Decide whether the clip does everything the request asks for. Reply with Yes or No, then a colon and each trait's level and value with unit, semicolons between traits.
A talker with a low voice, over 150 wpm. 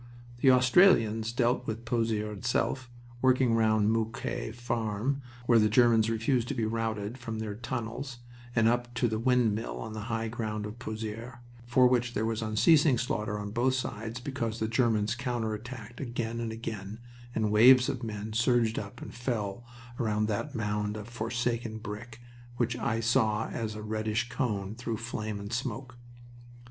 Yes: low, 115 Hz; average, 165 wpm